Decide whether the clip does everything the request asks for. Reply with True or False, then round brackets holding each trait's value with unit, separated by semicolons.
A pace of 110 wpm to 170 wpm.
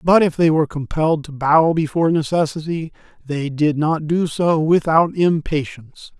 True (155 wpm)